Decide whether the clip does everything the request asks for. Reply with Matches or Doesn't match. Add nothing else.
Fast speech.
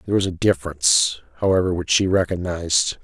Doesn't match